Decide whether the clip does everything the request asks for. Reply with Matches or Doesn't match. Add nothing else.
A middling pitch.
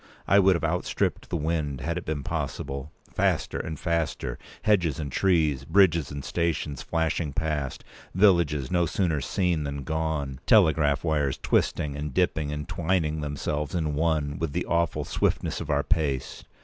Doesn't match